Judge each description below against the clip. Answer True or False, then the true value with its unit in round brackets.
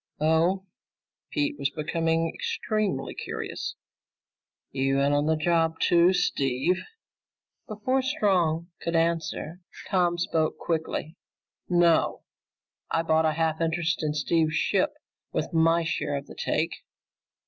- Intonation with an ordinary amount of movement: False (1.9 semitones)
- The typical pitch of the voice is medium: True (165 Hz)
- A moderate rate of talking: False (120 wpm)